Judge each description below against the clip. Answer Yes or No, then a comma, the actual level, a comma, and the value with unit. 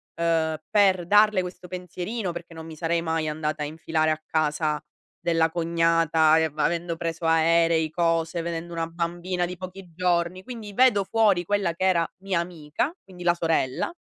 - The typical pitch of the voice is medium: Yes, medium, 170 Hz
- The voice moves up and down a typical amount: No, narrow, 2.0 semitones